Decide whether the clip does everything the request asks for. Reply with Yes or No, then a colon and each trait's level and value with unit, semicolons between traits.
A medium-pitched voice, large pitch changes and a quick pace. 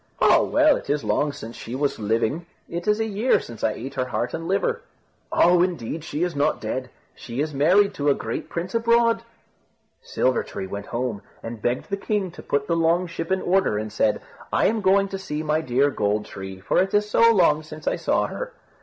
Yes: medium, 155 Hz; wide, 7.8 semitones; fast, 220 wpm